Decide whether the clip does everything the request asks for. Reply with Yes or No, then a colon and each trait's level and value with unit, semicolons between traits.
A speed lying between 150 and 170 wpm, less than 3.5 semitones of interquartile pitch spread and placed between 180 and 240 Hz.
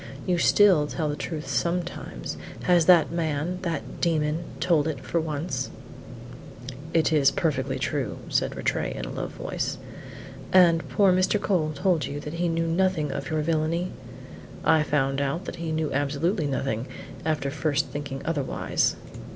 No: average, 155 wpm; average, 2.9 semitones; medium, 160 Hz